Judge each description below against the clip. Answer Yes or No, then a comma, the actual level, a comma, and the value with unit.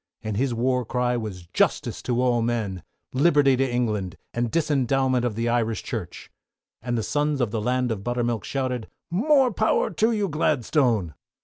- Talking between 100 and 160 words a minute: No, average, 170 wpm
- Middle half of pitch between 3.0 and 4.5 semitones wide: Yes, average, 3.3 semitones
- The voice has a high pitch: No, low, 125 Hz